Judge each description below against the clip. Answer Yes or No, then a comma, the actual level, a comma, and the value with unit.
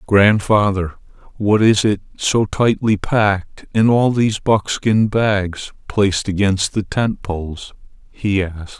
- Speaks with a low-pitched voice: Yes, low, 100 Hz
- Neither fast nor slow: No, slow, 130 wpm